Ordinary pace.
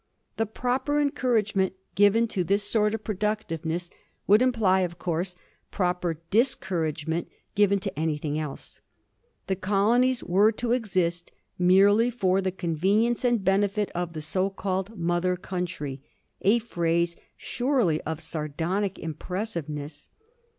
No: slow, 125 wpm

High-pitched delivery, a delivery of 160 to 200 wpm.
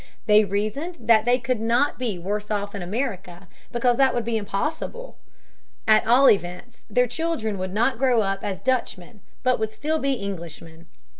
Yes: high, 220 Hz; average, 170 wpm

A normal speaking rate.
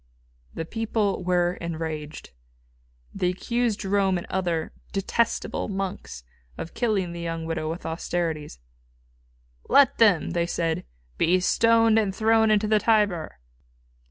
No: slow, 125 wpm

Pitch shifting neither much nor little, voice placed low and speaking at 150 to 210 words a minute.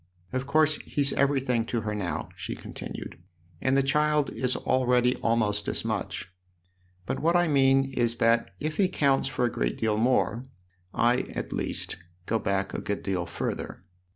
Yes: average, 4.2 semitones; low, 125 Hz; average, 175 wpm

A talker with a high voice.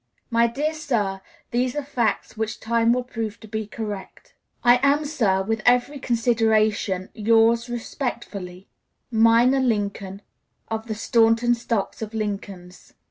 Yes: high, 225 Hz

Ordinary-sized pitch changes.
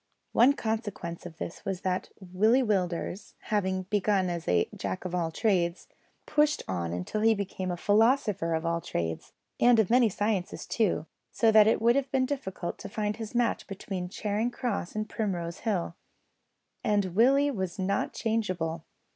Yes: average, 4.1 semitones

